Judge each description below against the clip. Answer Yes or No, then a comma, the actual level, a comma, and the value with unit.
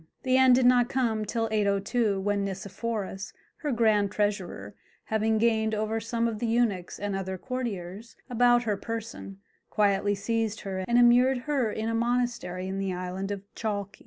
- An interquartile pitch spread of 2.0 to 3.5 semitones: Yes, average, 3.2 semitones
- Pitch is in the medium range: No, high, 220 Hz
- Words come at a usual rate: Yes, average, 165 wpm